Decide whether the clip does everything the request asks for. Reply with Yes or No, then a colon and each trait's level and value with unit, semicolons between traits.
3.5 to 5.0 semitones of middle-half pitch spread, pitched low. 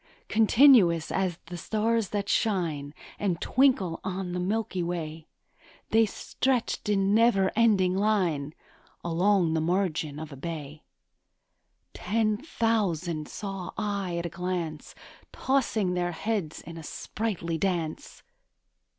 No: average, 4.3 semitones; medium, 185 Hz